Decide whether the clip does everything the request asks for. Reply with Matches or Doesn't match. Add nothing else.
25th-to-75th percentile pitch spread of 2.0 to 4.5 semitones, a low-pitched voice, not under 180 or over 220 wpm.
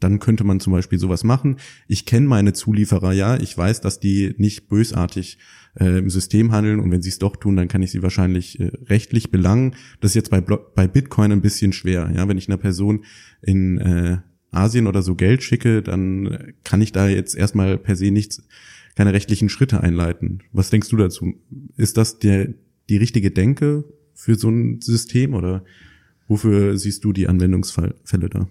Matches